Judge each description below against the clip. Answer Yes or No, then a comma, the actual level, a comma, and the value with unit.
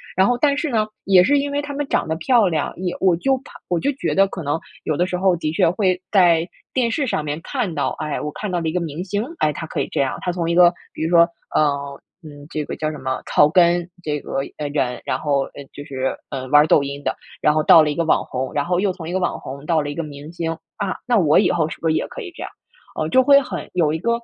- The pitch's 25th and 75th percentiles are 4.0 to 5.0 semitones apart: Yes, average, 4.5 semitones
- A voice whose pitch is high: No, medium, 170 Hz